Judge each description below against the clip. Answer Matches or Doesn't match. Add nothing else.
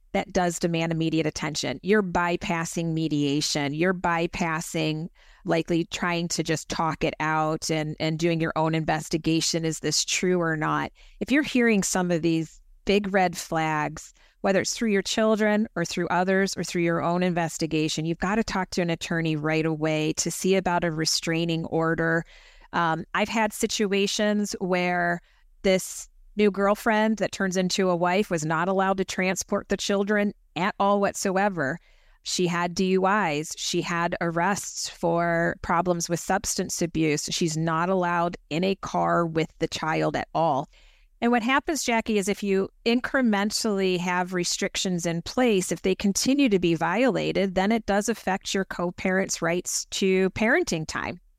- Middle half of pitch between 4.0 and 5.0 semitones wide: Doesn't match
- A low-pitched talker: Doesn't match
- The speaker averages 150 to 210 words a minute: Matches